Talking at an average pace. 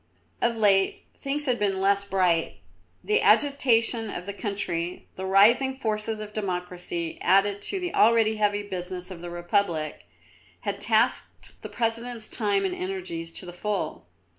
Yes: average, 150 wpm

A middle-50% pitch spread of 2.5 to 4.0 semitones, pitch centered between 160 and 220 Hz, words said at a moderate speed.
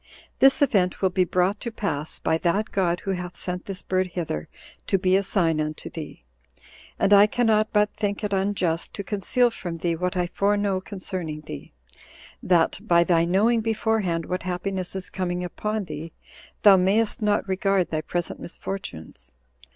Yes: average, 2.8 semitones; medium, 185 Hz; average, 170 wpm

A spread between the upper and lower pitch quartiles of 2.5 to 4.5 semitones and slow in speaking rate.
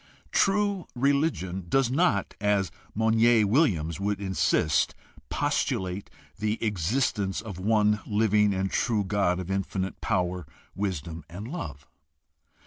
Yes: average, 3.3 semitones; slow, 115 wpm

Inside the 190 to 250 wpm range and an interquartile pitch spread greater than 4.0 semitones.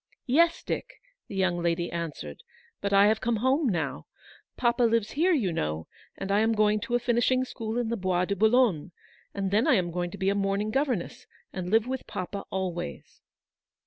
Yes: average, 195 wpm; average, 4.9 semitones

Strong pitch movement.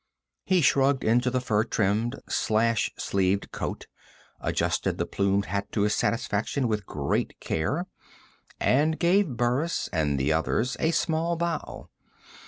Yes: wide, 6.8 semitones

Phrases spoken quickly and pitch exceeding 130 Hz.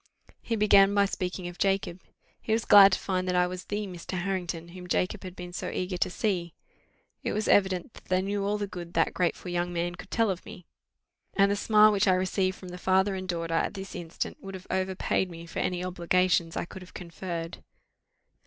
Yes: fast, 220 wpm; medium, 185 Hz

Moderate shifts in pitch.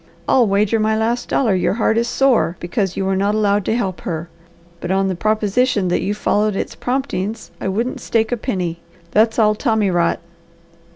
Yes: average, 3.0 semitones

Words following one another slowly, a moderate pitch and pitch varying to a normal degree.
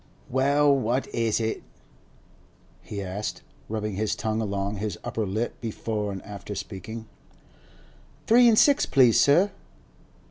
No: slow, 130 wpm; low, 110 Hz; average, 4.3 semitones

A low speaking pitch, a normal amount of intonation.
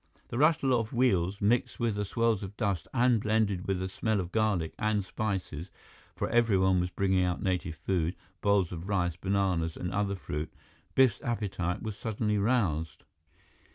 Yes: low, 100 Hz; average, 3.4 semitones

